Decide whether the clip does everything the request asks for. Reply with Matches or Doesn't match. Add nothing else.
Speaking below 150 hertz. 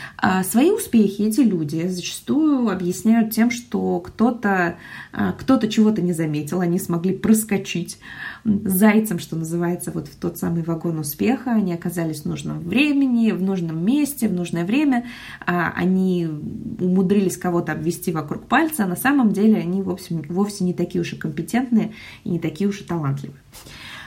Doesn't match